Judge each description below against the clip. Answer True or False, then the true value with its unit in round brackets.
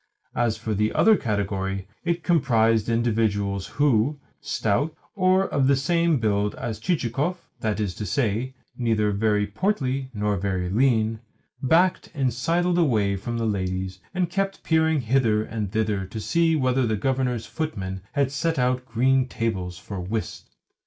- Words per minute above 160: False (150 wpm)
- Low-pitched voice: True (115 Hz)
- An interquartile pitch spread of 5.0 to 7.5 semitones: True (5.4 semitones)